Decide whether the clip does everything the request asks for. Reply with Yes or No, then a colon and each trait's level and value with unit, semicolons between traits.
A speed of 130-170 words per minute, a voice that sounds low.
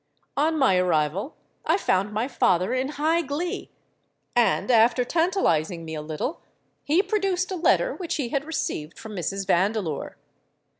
No: average, 150 wpm; high, 245 Hz